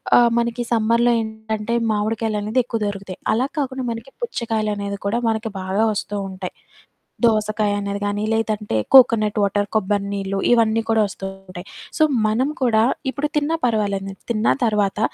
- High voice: Yes, high, 215 Hz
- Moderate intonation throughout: No, narrow, 2.2 semitones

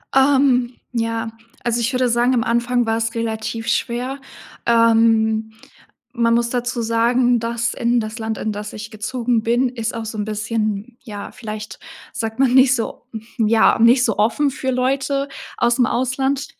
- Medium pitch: No, high, 235 Hz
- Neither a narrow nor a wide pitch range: No, narrow, 1.9 semitones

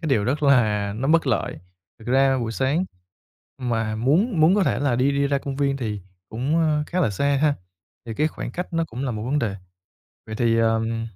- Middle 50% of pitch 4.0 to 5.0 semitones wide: Yes, average, 4.7 semitones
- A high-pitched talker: No, low, 135 Hz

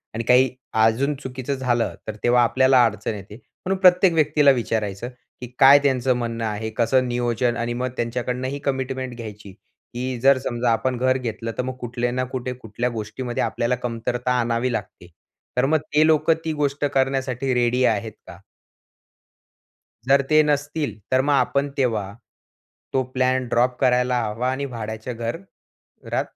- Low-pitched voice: Yes, low, 125 Hz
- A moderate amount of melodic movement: No, narrow, 2.3 semitones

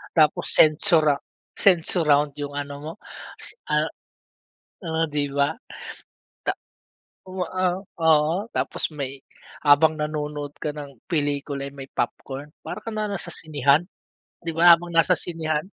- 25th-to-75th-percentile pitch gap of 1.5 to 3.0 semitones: Yes, narrow, 2.6 semitones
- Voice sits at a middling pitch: Yes, medium, 150 Hz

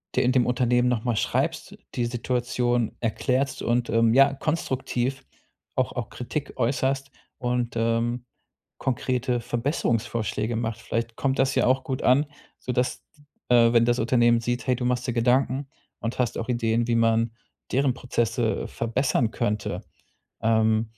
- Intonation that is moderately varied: No, narrow, 1.8 semitones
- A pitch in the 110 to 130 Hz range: Yes, low, 120 Hz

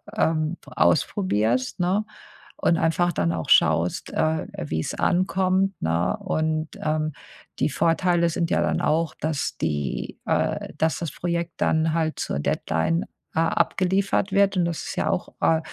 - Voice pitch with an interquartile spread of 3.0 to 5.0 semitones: No, narrow, 2.6 semitones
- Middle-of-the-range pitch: Yes, medium, 160 Hz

